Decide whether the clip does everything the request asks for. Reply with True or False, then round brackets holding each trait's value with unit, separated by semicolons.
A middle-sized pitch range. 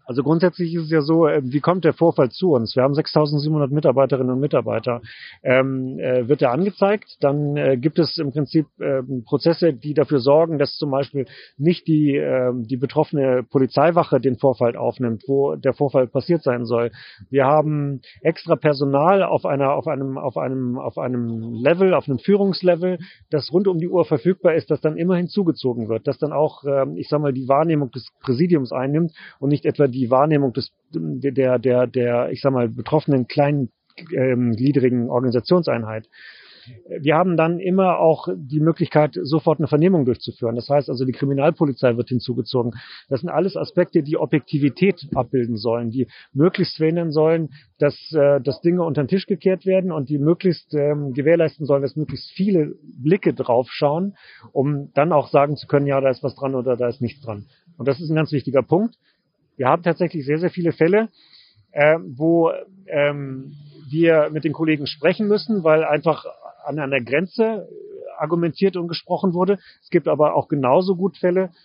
True (3.9 semitones)